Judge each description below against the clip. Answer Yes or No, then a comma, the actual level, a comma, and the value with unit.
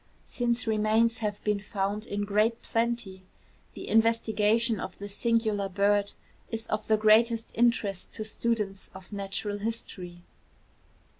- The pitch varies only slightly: Yes, narrow, 2.0 semitones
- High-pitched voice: Yes, high, 215 Hz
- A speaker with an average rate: No, slow, 130 wpm